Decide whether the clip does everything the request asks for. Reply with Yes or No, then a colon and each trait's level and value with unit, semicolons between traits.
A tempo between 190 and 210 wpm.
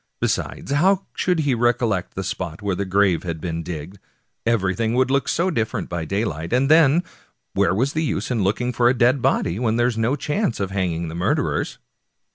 Yes: average, 200 wpm